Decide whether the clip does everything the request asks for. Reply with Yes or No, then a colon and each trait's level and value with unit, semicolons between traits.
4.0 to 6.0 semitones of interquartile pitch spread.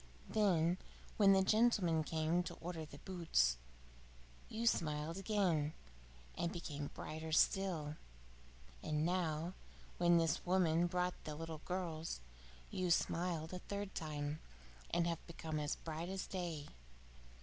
No: average, 2.7 semitones